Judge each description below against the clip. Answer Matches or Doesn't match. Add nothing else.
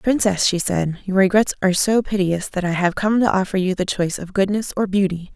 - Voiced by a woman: Matches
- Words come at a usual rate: Doesn't match